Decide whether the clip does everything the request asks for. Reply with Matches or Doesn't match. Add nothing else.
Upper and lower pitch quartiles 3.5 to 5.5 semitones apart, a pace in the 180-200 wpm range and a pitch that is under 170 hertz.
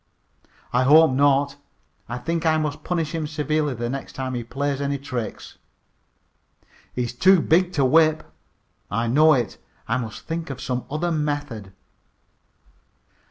Doesn't match